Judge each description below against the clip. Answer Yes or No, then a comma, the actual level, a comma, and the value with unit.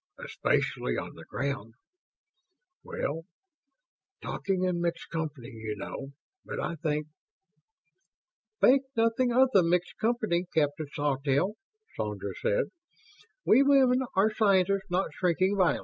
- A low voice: No, medium, 180 Hz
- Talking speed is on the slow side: Yes, slow, 120 wpm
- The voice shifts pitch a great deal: Yes, wide, 6.8 semitones